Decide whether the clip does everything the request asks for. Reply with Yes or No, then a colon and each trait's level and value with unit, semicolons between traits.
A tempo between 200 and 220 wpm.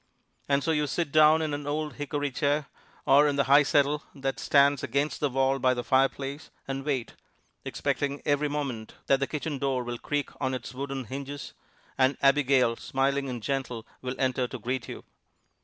No: average, 185 wpm